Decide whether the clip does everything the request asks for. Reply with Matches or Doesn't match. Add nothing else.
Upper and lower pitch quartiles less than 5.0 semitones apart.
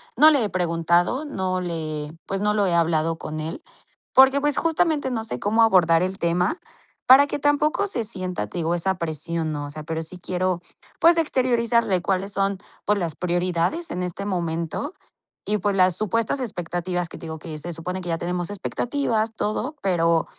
Doesn't match